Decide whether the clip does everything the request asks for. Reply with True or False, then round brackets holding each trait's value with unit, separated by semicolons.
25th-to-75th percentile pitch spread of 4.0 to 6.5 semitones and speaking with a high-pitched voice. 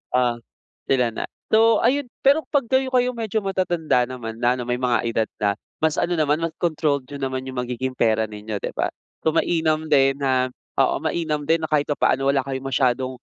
False (4.9 semitones; 140 Hz)